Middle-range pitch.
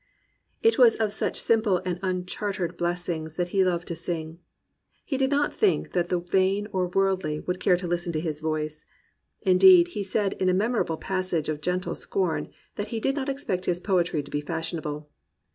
Yes: medium, 180 Hz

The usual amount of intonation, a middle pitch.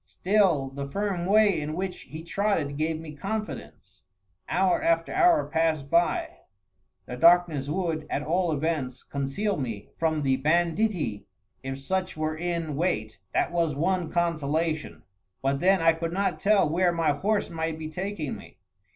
Yes: average, 3.8 semitones; medium, 165 Hz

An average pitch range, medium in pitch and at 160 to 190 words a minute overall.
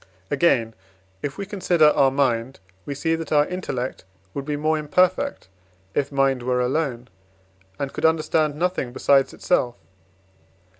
No: average, 3.5 semitones; medium, 145 Hz; average, 140 wpm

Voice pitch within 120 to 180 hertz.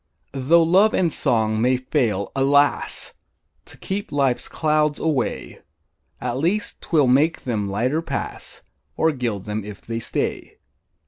Yes: low, 135 Hz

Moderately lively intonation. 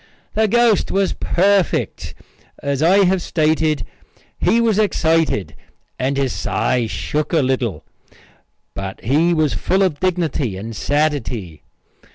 No: wide, 6.4 semitones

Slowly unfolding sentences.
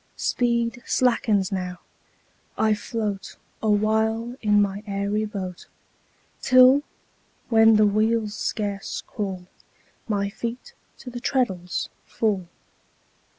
Yes: slow, 100 wpm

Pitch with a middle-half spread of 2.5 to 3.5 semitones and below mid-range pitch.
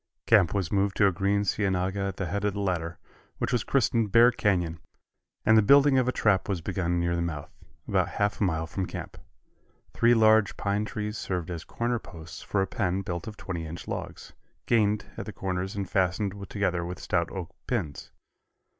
Yes: average, 3.2 semitones; very low, 95 Hz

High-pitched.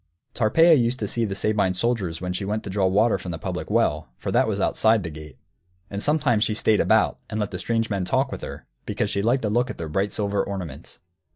No: low, 105 Hz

